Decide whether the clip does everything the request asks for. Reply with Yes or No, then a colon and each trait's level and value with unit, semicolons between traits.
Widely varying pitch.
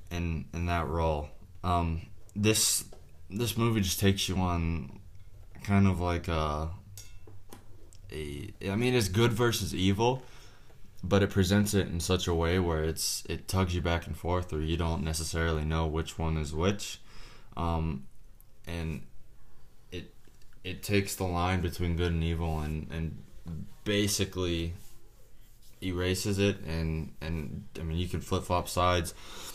No: average, 3.5 semitones